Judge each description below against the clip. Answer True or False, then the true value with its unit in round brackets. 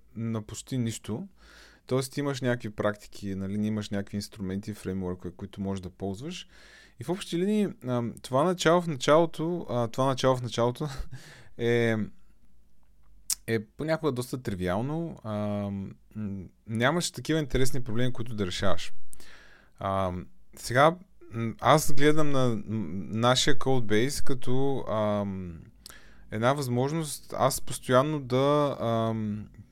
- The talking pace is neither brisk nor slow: False (105 wpm)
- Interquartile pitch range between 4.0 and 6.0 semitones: True (5.2 semitones)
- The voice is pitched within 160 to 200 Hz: False (120 Hz)